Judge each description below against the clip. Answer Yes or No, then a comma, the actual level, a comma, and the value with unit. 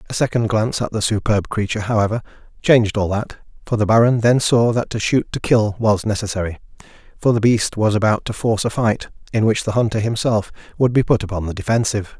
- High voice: No, low, 110 Hz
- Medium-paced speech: No, fast, 210 wpm